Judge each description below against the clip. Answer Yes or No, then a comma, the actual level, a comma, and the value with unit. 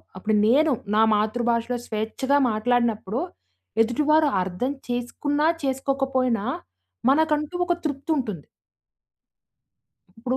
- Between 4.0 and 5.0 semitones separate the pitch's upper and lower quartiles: Yes, average, 4.4 semitones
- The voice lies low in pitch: No, high, 245 Hz